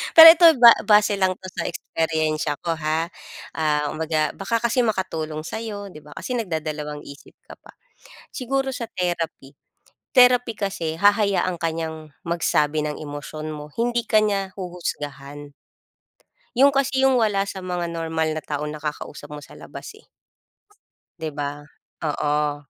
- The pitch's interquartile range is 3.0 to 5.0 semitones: No, wide, 5.4 semitones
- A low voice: No, medium, 165 Hz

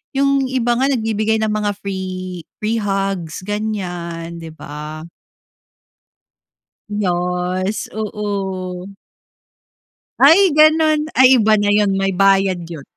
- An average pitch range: Yes, average, 3.4 semitones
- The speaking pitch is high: Yes, high, 195 Hz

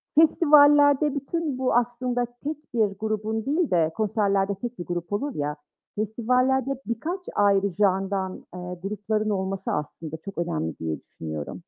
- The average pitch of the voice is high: Yes, high, 215 Hz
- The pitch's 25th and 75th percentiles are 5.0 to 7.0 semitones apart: Yes, wide, 5.6 semitones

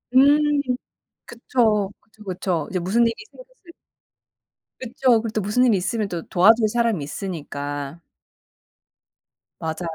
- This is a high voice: Yes, high, 210 Hz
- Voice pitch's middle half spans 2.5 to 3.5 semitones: No, average, 5.0 semitones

